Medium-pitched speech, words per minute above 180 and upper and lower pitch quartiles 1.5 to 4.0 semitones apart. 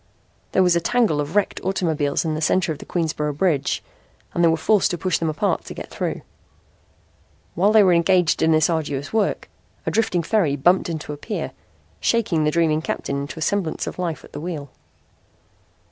Yes: medium, 165 Hz; average, 195 wpm; average, 3.4 semitones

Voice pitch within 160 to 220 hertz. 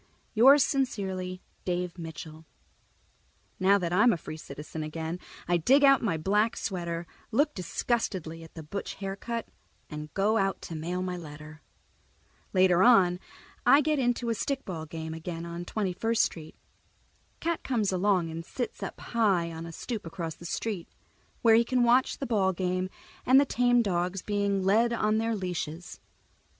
Yes: medium, 185 Hz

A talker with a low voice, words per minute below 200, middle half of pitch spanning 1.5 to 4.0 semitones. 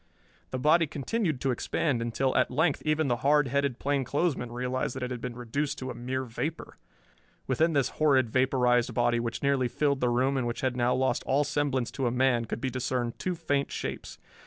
No: low, 130 Hz; fast, 205 wpm; narrow, 2.5 semitones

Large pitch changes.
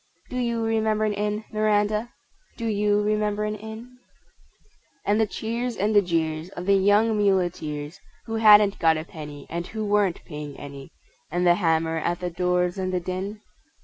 No: average, 3.6 semitones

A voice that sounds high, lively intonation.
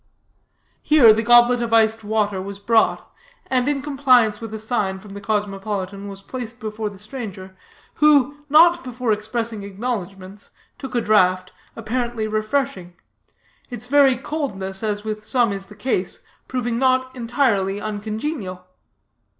No: high, 220 Hz; average, 3.8 semitones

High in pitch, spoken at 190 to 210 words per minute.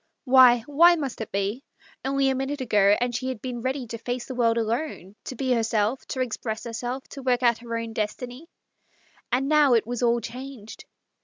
Yes: high, 245 Hz; average, 200 wpm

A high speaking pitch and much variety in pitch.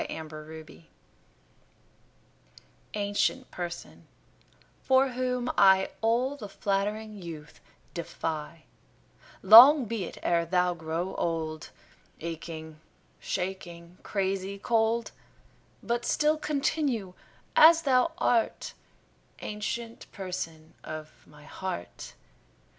Yes: high, 195 Hz; wide, 6.1 semitones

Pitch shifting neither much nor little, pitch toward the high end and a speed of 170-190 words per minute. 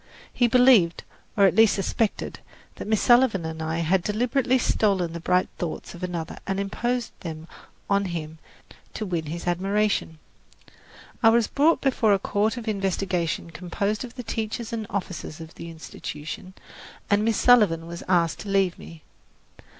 No: average, 4.8 semitones; high, 195 Hz; average, 160 wpm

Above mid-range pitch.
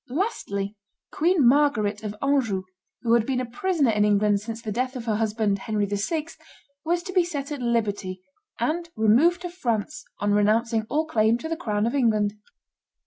Yes: high, 230 Hz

